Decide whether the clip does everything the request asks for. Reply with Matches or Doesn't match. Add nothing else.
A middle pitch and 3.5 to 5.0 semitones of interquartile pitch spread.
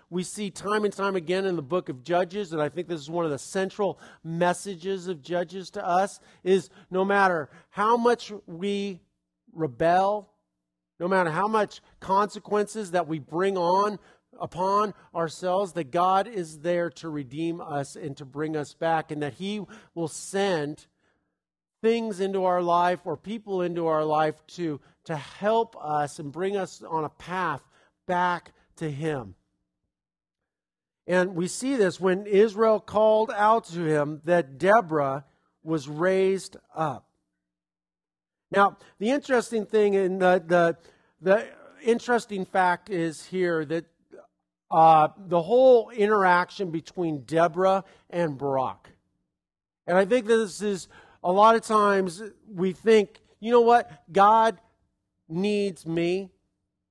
Matches